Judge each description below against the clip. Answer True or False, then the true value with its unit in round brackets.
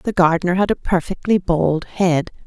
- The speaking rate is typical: True (170 wpm)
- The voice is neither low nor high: True (180 Hz)